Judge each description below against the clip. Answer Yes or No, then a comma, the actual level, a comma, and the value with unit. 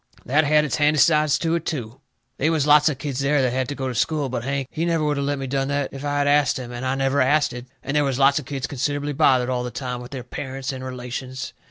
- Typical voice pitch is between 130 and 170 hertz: Yes, medium, 140 Hz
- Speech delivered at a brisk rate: Yes, fast, 280 wpm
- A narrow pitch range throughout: Yes, narrow, 2.2 semitones